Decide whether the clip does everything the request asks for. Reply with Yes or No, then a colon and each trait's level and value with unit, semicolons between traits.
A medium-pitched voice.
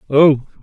Yes: medium, 145 Hz